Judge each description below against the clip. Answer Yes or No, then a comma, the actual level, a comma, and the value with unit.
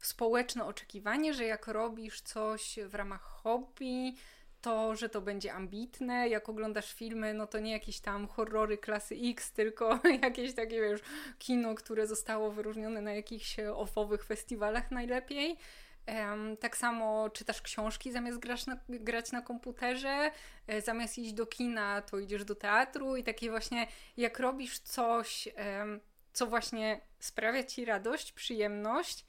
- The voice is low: No, high, 225 Hz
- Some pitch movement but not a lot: No, narrow, 2.2 semitones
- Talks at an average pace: Yes, average, 135 wpm